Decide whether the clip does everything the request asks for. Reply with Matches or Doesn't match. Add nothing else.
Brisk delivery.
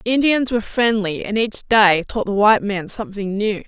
Matches